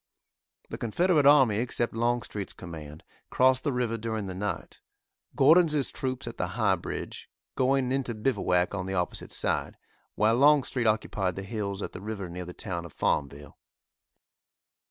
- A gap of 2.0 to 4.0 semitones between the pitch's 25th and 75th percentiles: No, wide, 5.5 semitones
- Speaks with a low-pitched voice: Yes, low, 110 Hz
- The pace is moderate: Yes, average, 155 wpm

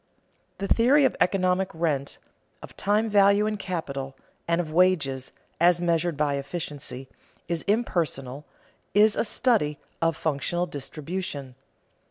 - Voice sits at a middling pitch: Yes, medium, 170 Hz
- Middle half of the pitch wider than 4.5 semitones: Yes, average, 5.3 semitones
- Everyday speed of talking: No, slow, 125 wpm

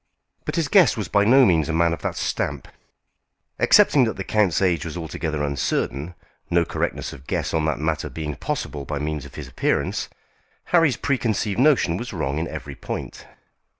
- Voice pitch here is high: No, very low, 85 Hz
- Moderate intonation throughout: No, wide, 6.6 semitones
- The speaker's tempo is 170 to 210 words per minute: Yes, average, 185 wpm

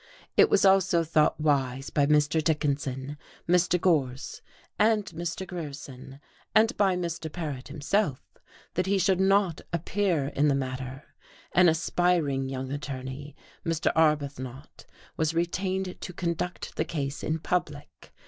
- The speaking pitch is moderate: Yes, medium, 155 Hz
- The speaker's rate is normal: No, slow, 130 wpm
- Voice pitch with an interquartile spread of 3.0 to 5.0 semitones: Yes, average, 4.4 semitones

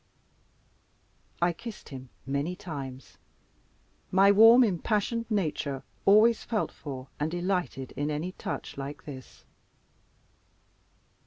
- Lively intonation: Yes, wide, 6.8 semitones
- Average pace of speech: No, slow, 100 wpm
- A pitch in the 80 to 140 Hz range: No, medium, 175 Hz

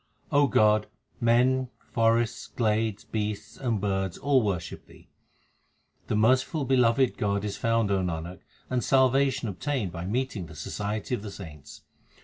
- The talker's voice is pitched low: Yes, low, 110 Hz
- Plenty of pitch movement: No, average, 4.3 semitones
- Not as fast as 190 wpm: Yes, average, 140 wpm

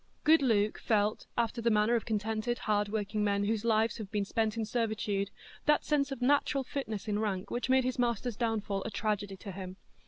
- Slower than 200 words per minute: No, fast, 205 wpm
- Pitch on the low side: No, high, 220 Hz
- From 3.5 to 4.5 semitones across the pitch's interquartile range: No, narrow, 2.6 semitones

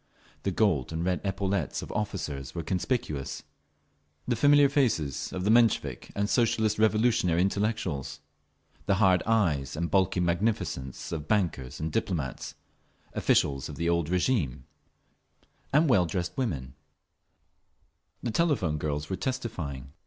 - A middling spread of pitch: No, wide, 6.3 semitones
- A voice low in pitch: Yes, very low, 90 Hz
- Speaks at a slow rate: Yes, slow, 130 wpm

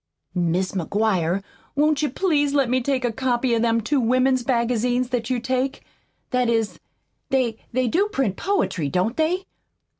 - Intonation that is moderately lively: Yes, average, 3.2 semitones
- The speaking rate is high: No, average, 160 wpm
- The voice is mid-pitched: No, very high, 250 Hz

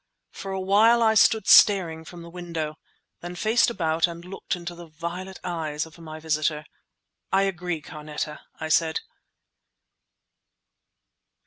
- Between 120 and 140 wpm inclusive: Yes, slow, 135 wpm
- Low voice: No, medium, 170 Hz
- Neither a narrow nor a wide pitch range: Yes, average, 3.2 semitones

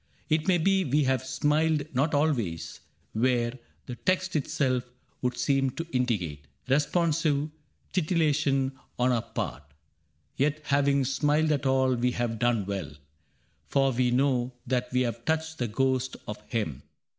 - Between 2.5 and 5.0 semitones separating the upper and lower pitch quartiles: Yes, average, 3.6 semitones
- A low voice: Yes, low, 130 Hz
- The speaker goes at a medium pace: Yes, average, 145 wpm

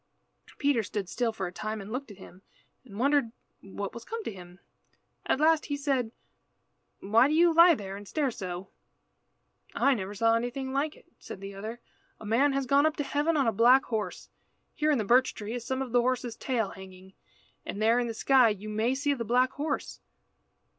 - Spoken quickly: Yes, fast, 210 wpm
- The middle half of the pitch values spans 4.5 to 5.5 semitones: Yes, average, 5.0 semitones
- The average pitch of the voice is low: No, high, 240 Hz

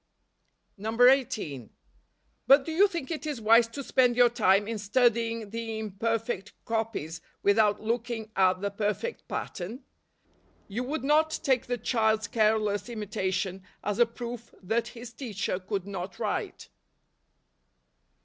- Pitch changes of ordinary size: Yes, average, 3.2 semitones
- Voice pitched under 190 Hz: No, high, 225 Hz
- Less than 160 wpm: Yes, average, 140 wpm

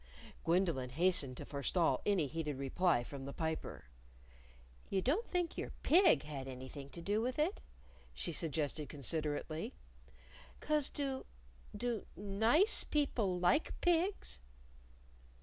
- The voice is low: No, medium, 175 Hz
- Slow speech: Yes, slow, 120 wpm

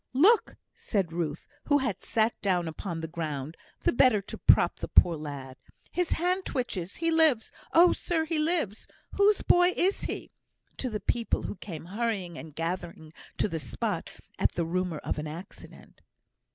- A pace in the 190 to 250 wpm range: No, average, 170 wpm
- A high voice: Yes, high, 195 Hz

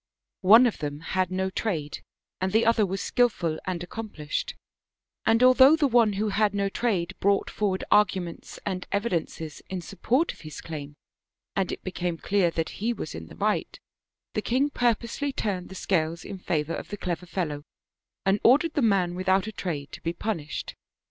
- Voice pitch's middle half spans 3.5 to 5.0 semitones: Yes, average, 4.6 semitones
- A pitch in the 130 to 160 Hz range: No, high, 190 Hz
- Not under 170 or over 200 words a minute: Yes, average, 180 wpm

